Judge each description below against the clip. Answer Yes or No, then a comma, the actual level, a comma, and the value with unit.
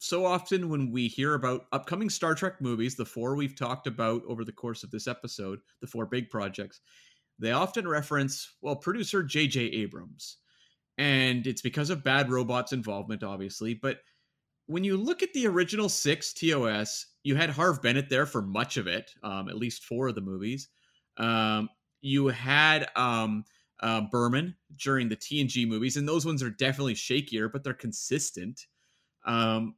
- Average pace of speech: Yes, average, 170 wpm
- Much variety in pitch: No, average, 4.6 semitones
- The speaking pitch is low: Yes, low, 130 Hz